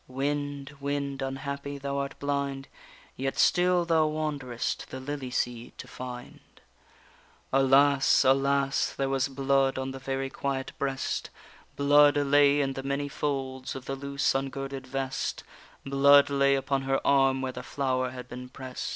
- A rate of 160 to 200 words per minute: No, average, 150 wpm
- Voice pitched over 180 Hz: No, low, 135 Hz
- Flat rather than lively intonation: Yes, narrow, 1.0 semitones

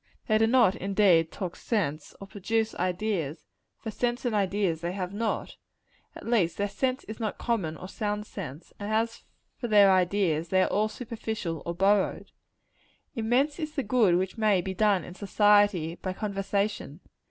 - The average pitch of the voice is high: Yes, high, 205 Hz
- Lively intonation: No, average, 3.3 semitones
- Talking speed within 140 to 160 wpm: No, average, 170 wpm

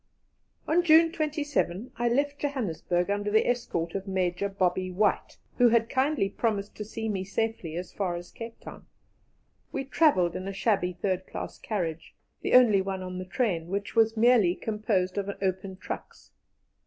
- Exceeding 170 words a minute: No, average, 165 wpm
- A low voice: No, high, 200 Hz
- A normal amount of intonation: Yes, average, 4.4 semitones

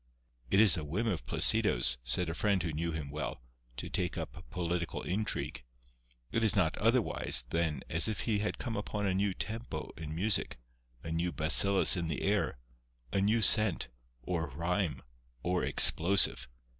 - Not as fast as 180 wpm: Yes, average, 170 wpm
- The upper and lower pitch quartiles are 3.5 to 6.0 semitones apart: Yes, average, 4.1 semitones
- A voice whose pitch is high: No, very low, 90 Hz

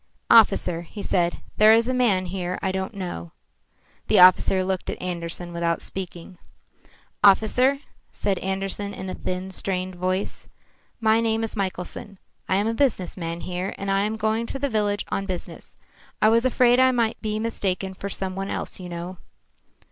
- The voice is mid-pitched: No, high, 195 Hz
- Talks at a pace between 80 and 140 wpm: No, average, 175 wpm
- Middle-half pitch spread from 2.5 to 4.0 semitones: Yes, average, 3.2 semitones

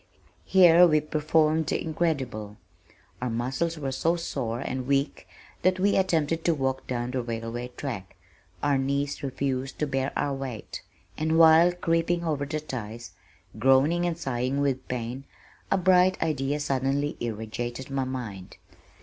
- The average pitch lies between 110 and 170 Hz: Yes, medium, 140 Hz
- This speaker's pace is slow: No, average, 150 wpm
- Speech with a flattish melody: No, average, 4.2 semitones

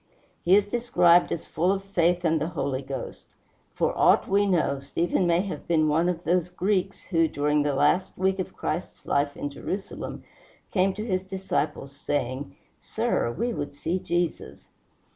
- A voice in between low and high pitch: Yes, medium, 175 Hz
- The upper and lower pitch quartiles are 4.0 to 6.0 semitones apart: Yes, average, 4.3 semitones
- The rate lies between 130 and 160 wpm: No, average, 170 wpm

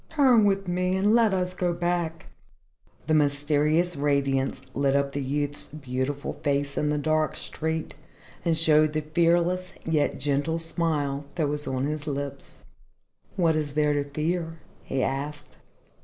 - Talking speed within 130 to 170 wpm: Yes, average, 150 wpm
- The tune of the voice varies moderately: Yes, average, 3.1 semitones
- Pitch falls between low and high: Yes, medium, 155 Hz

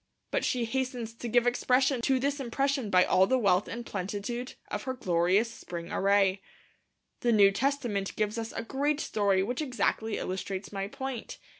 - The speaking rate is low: No, average, 170 wpm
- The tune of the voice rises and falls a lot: No, average, 4.4 semitones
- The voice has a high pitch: Yes, high, 230 Hz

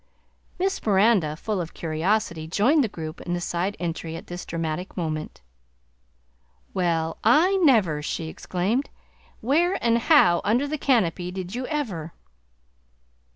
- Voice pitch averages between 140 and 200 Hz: Yes, medium, 185 Hz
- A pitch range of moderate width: No, wide, 6.7 semitones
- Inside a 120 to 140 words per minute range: Yes, slow, 135 wpm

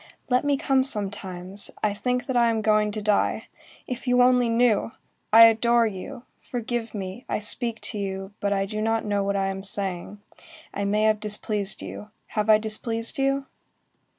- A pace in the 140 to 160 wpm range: No, average, 180 wpm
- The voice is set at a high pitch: Yes, high, 215 Hz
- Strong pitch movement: No, average, 2.9 semitones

